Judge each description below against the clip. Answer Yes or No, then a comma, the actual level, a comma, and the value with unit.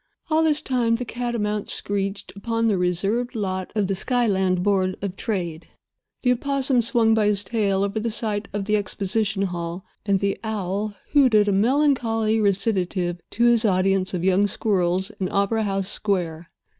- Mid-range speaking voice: No, high, 205 Hz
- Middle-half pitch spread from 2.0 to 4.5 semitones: Yes, average, 3.1 semitones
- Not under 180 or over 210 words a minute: No, average, 165 wpm